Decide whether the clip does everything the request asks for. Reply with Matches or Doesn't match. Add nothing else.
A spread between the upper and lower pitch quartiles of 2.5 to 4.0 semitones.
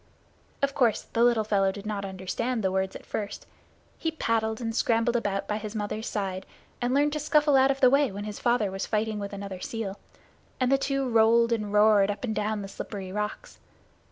Matches